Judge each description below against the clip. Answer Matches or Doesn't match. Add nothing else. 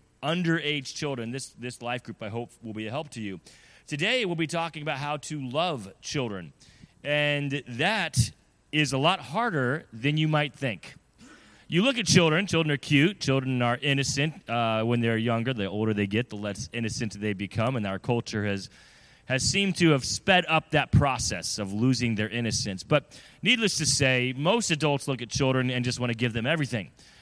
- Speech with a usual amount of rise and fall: Matches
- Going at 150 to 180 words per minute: Doesn't match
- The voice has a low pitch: Matches